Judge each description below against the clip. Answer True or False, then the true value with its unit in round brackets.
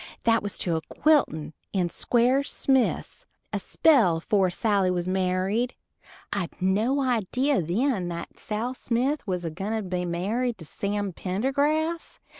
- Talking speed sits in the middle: True (145 wpm)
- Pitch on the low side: False (205 Hz)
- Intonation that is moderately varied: False (5.8 semitones)